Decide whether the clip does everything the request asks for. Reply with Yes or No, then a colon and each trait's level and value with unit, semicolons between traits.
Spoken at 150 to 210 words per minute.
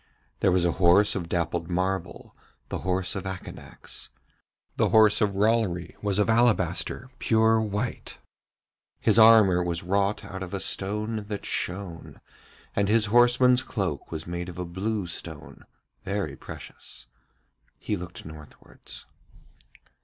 No: slow, 135 wpm